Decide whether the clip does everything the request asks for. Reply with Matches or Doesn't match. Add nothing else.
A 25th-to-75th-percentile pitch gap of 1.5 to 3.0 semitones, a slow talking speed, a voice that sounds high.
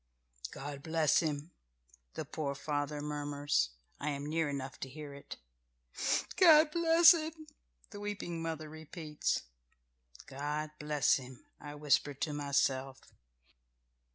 Doesn't match